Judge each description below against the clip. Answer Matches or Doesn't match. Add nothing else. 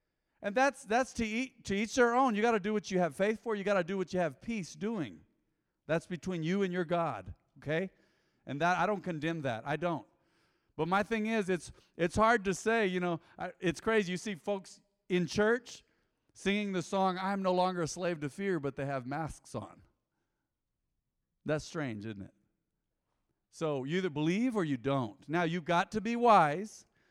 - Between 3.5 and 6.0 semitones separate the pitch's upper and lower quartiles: Matches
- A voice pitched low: Doesn't match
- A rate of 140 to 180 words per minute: Doesn't match